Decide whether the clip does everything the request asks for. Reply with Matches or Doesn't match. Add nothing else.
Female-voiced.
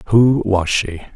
Doesn't match